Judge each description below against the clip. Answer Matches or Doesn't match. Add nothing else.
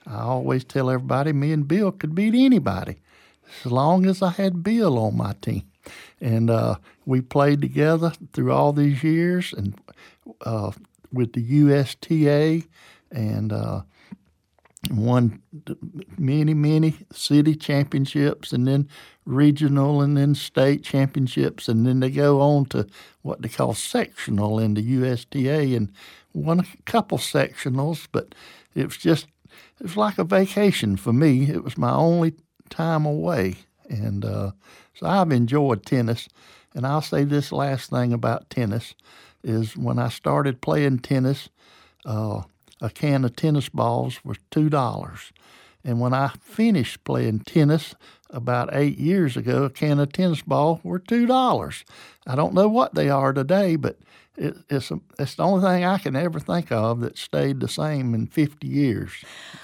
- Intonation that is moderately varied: Matches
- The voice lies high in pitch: Doesn't match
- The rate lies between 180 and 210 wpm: Doesn't match